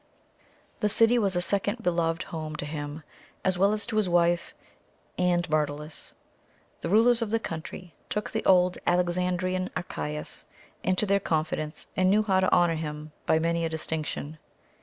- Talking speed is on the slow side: No, average, 160 wpm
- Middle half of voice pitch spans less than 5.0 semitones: Yes, average, 3.6 semitones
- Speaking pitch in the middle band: Yes, medium, 175 Hz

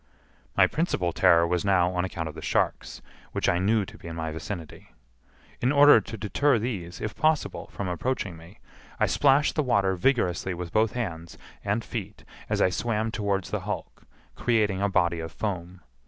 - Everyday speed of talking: Yes, average, 185 wpm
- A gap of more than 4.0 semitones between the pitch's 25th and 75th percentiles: Yes, average, 4.4 semitones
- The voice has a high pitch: No, low, 100 Hz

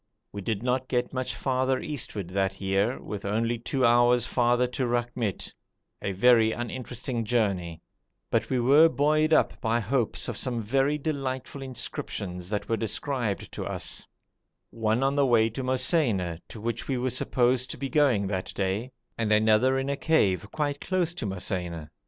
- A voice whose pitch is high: No, low, 120 Hz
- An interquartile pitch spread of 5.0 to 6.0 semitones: No, average, 3.9 semitones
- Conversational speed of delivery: Yes, average, 165 wpm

